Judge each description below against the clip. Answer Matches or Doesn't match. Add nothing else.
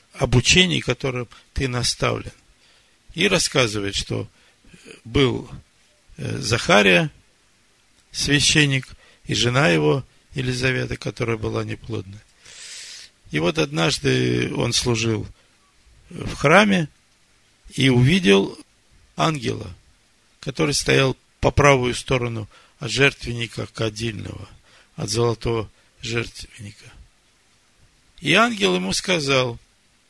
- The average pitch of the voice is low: Matches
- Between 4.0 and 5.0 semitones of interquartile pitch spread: Matches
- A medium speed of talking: Doesn't match